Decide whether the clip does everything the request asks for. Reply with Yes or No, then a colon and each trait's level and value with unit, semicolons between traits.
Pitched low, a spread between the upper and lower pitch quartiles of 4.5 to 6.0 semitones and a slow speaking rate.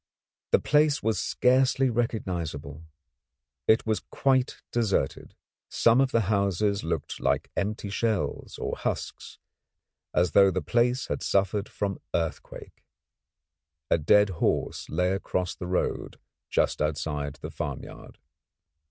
Yes: low, 100 Hz; average, 5.0 semitones; slow, 120 wpm